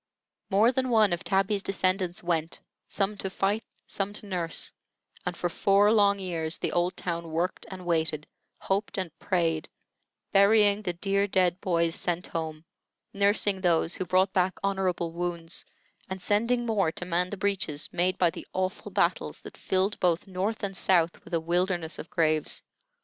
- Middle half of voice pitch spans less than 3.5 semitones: Yes, average, 2.7 semitones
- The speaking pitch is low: No, medium, 185 Hz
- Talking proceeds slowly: No, average, 165 wpm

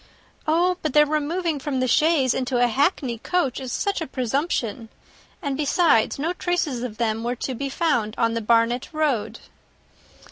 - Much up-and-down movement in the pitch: No, average, 4.7 semitones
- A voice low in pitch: No, very high, 270 Hz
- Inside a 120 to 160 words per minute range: No, average, 170 wpm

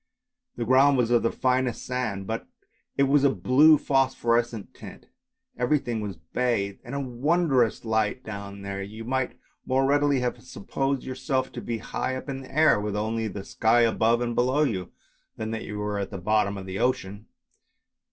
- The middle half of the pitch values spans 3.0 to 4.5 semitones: Yes, average, 3.9 semitones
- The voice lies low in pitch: Yes, low, 120 Hz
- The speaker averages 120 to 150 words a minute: No, average, 190 wpm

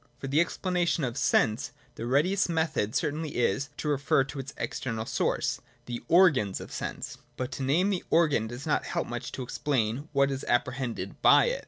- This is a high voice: No, low, 135 Hz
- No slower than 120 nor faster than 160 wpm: No, average, 195 wpm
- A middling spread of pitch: Yes, average, 4.6 semitones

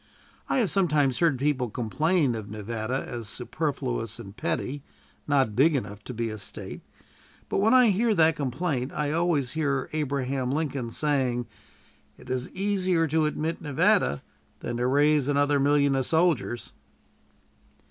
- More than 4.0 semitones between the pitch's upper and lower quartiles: Yes, average, 4.4 semitones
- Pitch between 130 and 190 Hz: Yes, medium, 140 Hz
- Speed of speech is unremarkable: Yes, average, 145 wpm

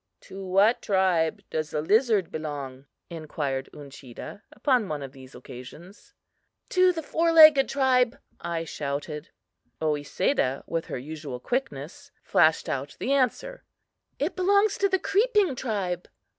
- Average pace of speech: No, slow, 130 wpm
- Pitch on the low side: No, medium, 180 Hz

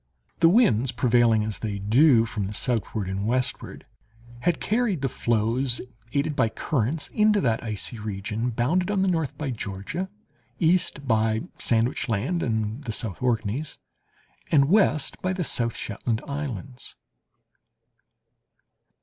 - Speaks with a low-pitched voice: Yes, low, 120 Hz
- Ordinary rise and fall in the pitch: No, wide, 5.7 semitones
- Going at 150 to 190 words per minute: No, slow, 135 wpm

